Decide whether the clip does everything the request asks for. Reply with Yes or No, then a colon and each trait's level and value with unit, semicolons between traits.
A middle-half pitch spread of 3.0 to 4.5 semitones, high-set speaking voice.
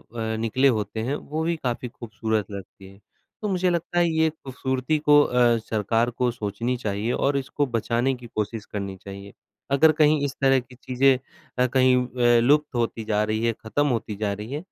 No: average, 4.0 semitones; low, 125 Hz